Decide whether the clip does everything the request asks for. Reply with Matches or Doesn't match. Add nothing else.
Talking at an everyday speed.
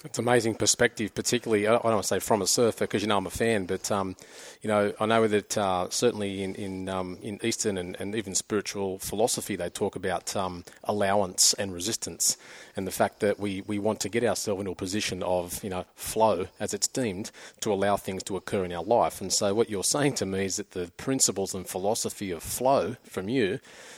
Doesn't match